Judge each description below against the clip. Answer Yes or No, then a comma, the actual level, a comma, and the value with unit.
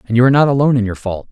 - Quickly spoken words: Yes, fast, 365 wpm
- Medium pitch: No, low, 120 Hz